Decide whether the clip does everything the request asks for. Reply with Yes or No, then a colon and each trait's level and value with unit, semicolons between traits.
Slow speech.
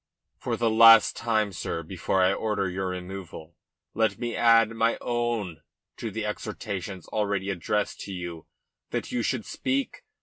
No: average, 155 wpm